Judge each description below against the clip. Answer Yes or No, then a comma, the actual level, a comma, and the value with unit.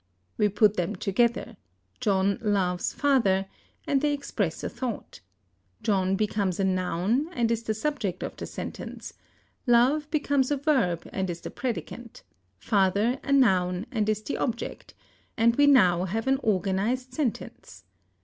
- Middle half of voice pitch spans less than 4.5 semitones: No, average, 5.2 semitones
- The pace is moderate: Yes, average, 150 wpm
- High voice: Yes, high, 215 Hz